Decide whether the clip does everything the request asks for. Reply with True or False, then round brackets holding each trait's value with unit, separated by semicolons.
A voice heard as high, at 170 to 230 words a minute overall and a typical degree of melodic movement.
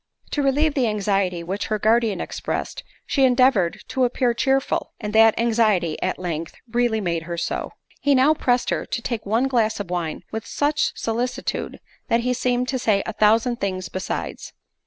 True (225 Hz; 180 wpm; 4.2 semitones)